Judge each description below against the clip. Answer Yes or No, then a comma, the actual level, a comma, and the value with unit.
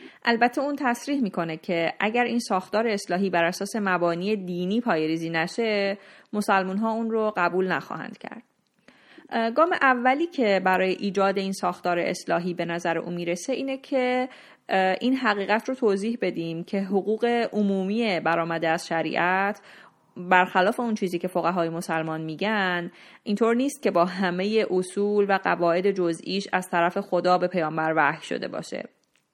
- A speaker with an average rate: Yes, average, 145 wpm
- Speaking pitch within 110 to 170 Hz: No, high, 195 Hz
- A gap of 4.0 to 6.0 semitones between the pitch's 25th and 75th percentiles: Yes, average, 4.3 semitones